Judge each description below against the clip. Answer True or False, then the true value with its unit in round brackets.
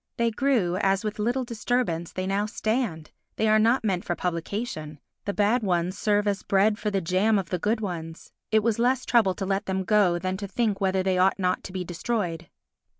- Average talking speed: False (210 wpm)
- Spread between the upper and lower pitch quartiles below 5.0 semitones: True (3.1 semitones)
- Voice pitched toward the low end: False (200 Hz)